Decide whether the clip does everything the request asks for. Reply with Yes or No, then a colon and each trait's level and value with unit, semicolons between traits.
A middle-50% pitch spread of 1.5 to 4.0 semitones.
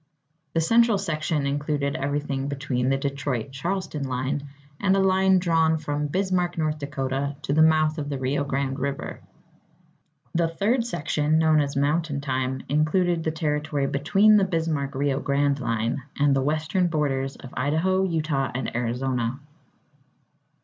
Yes: average, 3.0 semitones